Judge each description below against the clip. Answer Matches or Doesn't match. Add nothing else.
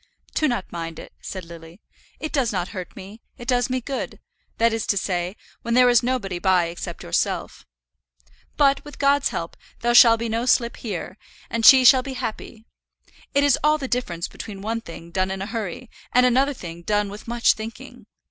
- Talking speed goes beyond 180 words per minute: Matches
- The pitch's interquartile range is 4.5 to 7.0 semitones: Matches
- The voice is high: Matches